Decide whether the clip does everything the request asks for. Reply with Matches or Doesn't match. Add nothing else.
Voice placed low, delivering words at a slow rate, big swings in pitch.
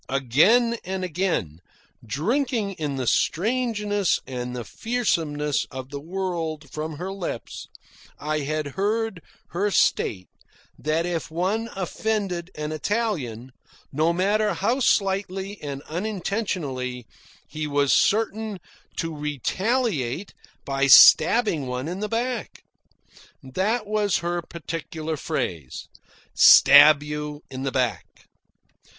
Doesn't match